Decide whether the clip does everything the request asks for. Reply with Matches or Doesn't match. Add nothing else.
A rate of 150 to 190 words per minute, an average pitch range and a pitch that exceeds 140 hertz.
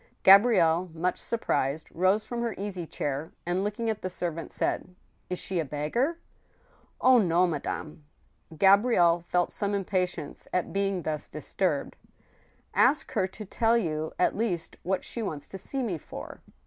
Matches